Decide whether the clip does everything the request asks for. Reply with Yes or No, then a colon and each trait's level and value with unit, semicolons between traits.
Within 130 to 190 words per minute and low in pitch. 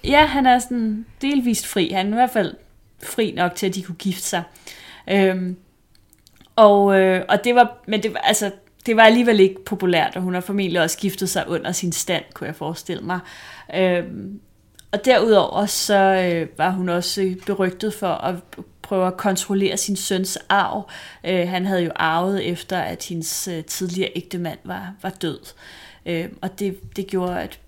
No: average, 185 wpm; high, 190 Hz